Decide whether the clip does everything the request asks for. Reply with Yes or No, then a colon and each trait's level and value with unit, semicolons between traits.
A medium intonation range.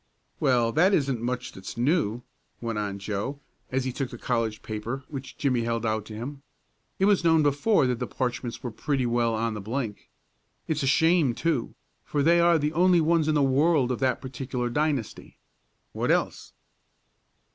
Yes: average, 4.4 semitones